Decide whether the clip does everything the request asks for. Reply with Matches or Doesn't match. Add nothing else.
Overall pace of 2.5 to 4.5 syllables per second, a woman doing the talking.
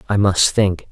Doesn't match